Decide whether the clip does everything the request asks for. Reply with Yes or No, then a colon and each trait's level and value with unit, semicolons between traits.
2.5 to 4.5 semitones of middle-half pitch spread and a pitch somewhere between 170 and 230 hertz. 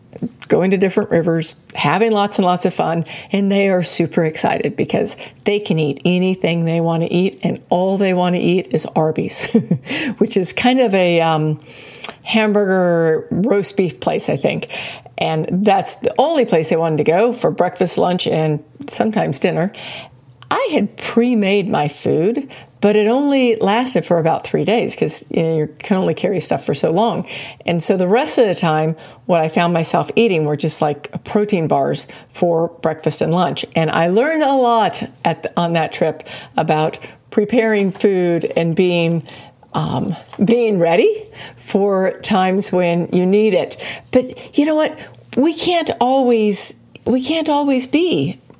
No: average, 5.2 semitones; medium, 185 Hz